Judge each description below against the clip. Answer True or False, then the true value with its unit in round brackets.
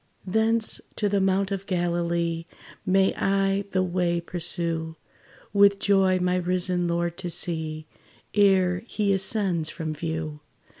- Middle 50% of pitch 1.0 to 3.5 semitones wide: True (2.4 semitones)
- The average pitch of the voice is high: False (180 Hz)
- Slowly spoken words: True (130 wpm)